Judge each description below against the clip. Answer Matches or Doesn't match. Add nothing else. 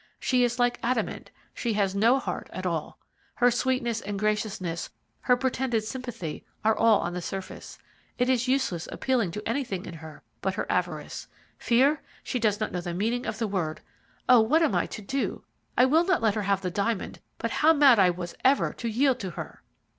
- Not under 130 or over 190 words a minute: Doesn't match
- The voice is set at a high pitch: Matches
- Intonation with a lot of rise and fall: Doesn't match